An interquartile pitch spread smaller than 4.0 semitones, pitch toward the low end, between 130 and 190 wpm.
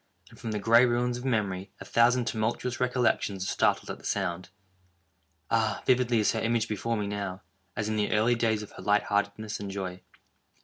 No: narrow, 2.6 semitones; low, 110 Hz; average, 200 wpm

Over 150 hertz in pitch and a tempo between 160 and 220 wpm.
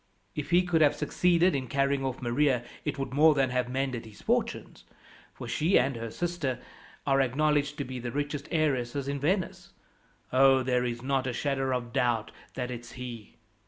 No: low, 135 Hz; average, 185 wpm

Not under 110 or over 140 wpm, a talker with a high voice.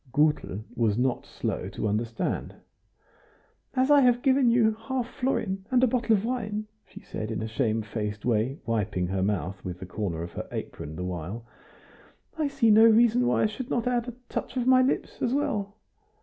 No: average, 190 wpm; high, 200 Hz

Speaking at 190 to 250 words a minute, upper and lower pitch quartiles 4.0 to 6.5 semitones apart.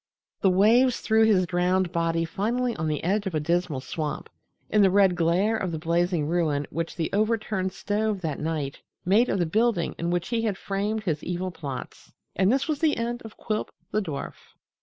Yes: average, 200 wpm; average, 4.5 semitones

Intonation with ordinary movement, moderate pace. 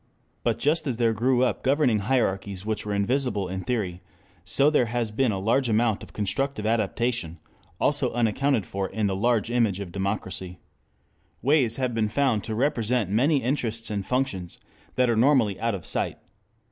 Yes: average, 4.1 semitones; average, 170 wpm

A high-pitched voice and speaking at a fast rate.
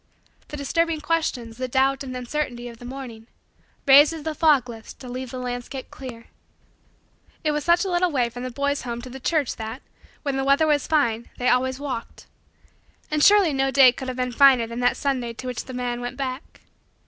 Yes: very high, 260 Hz; fast, 210 wpm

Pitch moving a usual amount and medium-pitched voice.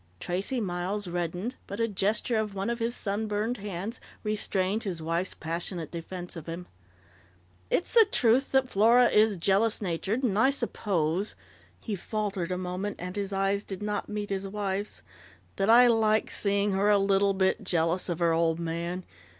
No: average, 3.2 semitones; high, 200 Hz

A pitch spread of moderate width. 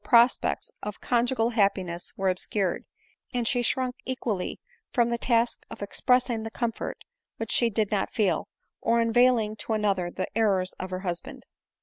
Yes: average, 3.6 semitones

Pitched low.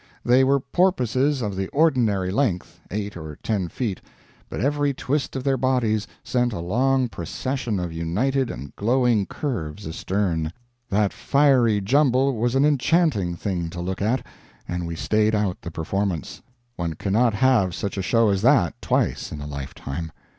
Yes: low, 105 Hz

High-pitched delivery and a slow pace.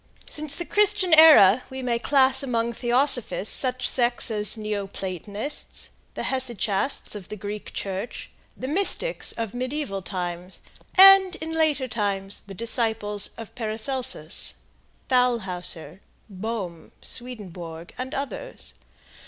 Yes: high, 235 Hz; slow, 120 wpm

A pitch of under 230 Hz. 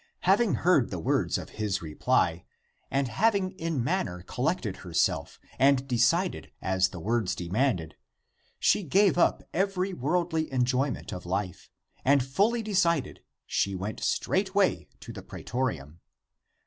Yes: low, 135 Hz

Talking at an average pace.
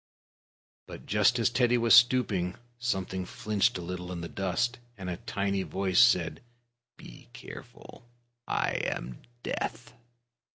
No: slow, 130 wpm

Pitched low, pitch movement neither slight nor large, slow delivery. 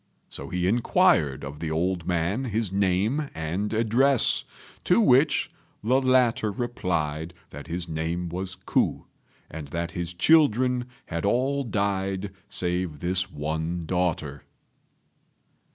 No: very low, 95 Hz; wide, 5.7 semitones; slow, 120 wpm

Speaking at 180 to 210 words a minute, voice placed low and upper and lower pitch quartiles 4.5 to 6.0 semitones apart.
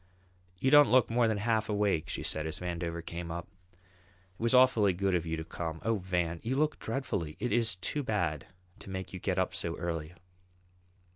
Yes: average, 200 wpm; very low, 95 Hz; average, 5.2 semitones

